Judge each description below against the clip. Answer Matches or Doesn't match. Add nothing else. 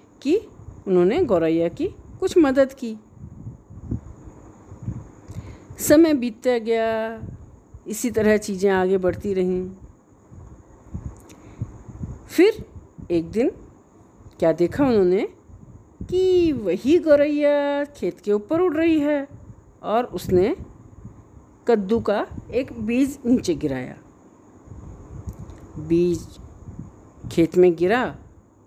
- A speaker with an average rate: Doesn't match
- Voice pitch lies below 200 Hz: Doesn't match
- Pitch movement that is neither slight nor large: Doesn't match